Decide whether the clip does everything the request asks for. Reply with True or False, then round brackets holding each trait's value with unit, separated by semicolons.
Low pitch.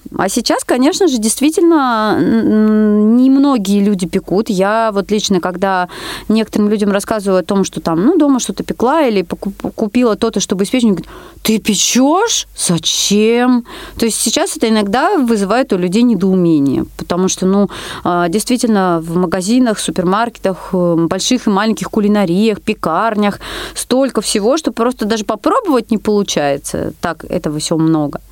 False (215 Hz)